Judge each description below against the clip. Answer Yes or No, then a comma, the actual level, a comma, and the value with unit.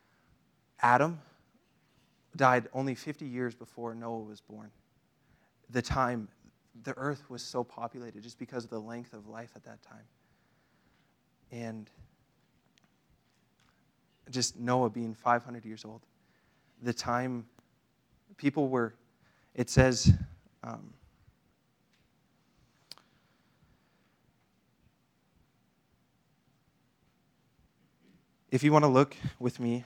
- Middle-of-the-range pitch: No, low, 120 Hz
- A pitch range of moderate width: No, narrow, 2.0 semitones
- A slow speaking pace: Yes, slow, 95 wpm